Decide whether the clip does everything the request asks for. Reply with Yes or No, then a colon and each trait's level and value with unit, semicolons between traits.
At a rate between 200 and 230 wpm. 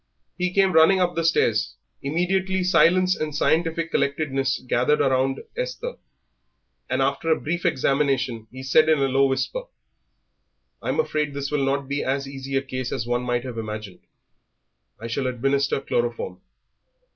No: average, 155 wpm